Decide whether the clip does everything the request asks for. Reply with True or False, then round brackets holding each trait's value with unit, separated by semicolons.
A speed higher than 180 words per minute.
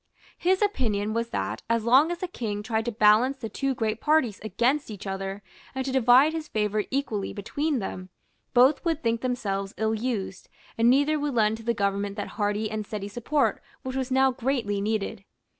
True (190 wpm)